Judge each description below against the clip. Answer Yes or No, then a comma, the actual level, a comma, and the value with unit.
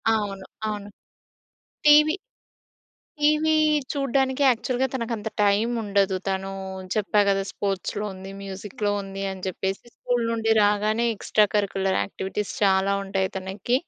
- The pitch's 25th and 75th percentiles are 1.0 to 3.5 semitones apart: Yes, average, 3.2 semitones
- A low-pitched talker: No, high, 205 Hz